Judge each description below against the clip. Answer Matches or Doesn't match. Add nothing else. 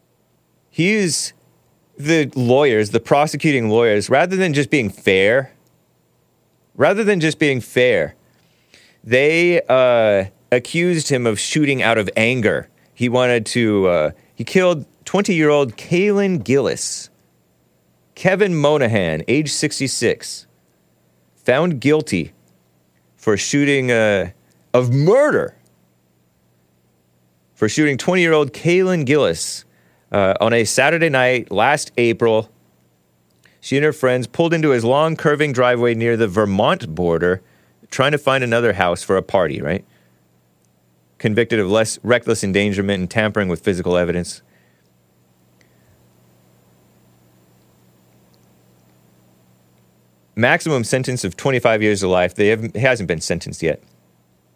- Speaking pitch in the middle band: Doesn't match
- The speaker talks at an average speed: Doesn't match